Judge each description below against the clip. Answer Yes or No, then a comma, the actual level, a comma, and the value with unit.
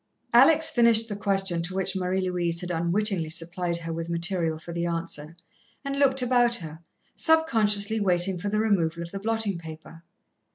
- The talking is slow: No, average, 170 wpm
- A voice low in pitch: No, medium, 185 Hz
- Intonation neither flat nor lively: Yes, average, 4.2 semitones